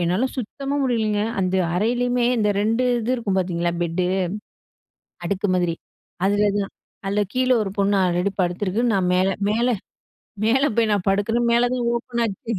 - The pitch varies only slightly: No, average, 4.1 semitones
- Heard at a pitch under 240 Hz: Yes, high, 210 Hz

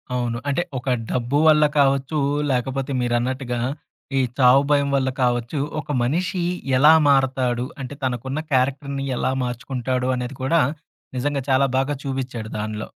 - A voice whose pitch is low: Yes, low, 130 Hz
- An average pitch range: No, narrow, 2.1 semitones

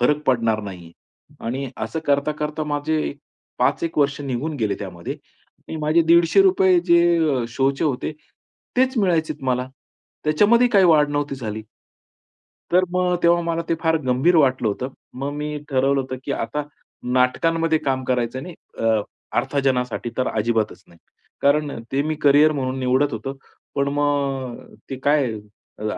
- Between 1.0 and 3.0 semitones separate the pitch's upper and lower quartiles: No, average, 3.9 semitones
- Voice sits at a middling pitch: Yes, medium, 145 Hz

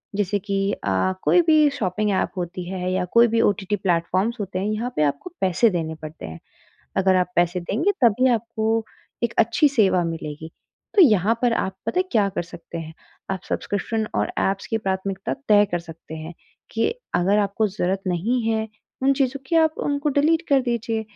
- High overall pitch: Yes, high, 205 Hz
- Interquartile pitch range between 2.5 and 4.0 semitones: No, average, 4.5 semitones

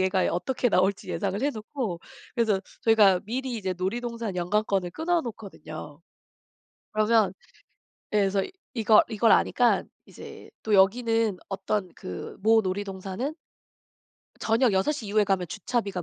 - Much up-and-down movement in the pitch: No, average, 3.3 semitones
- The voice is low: No, high, 210 Hz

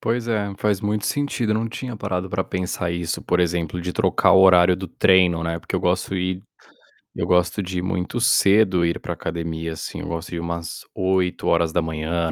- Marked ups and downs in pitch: No, narrow, 2.5 semitones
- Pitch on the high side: No, very low, 90 Hz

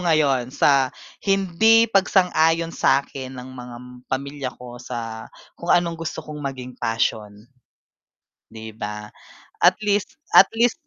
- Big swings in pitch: Yes, wide, 6.1 semitones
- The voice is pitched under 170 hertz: Yes, medium, 140 Hz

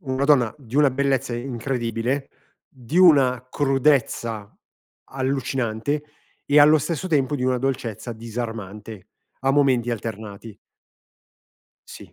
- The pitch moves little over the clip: No, average, 3.3 semitones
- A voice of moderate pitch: No, low, 130 Hz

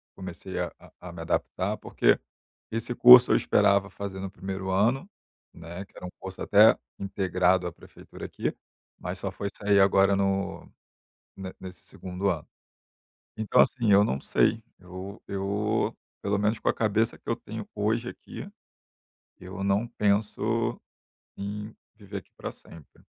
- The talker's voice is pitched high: No, low, 100 Hz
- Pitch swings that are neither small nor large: No, narrow, 2.1 semitones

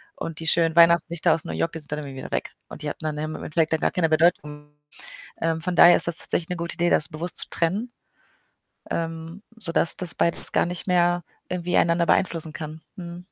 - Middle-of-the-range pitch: Yes, medium, 165 Hz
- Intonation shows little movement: Yes, narrow, 1.7 semitones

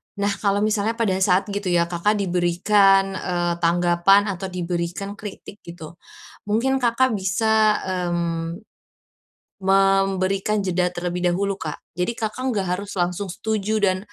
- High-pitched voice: Yes, high, 195 Hz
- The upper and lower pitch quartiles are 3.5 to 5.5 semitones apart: No, average, 2.7 semitones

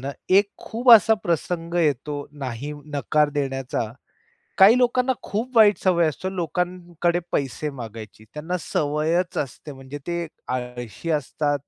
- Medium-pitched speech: Yes, medium, 155 Hz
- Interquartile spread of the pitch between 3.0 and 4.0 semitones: No, average, 4.6 semitones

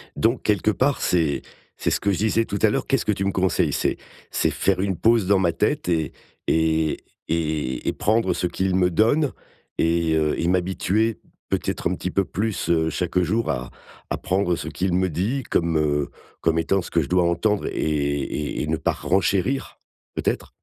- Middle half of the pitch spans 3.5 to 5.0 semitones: Yes, average, 4.2 semitones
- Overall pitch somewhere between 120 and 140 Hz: No, very low, 90 Hz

